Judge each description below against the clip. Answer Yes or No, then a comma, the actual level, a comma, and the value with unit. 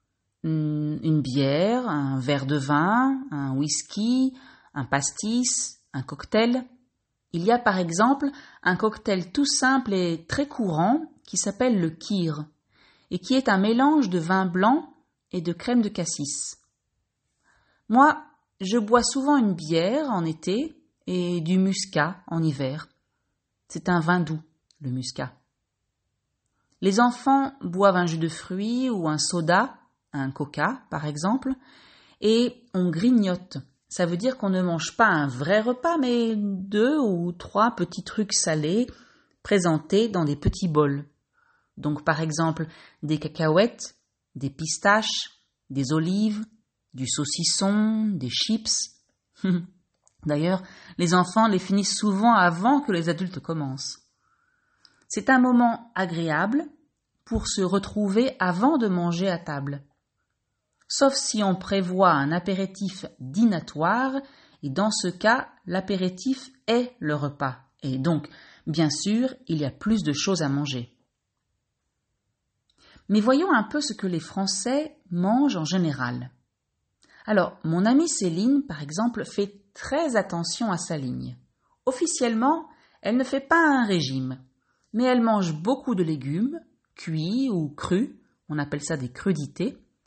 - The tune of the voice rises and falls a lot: Yes, wide, 7.4 semitones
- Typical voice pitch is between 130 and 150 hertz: No, medium, 185 Hz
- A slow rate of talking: Yes, slow, 135 wpm